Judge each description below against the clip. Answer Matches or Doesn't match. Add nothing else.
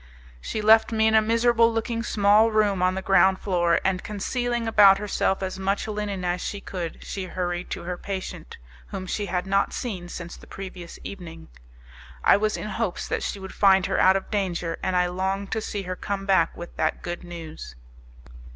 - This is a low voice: Doesn't match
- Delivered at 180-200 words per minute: Matches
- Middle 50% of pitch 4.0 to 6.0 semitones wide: Doesn't match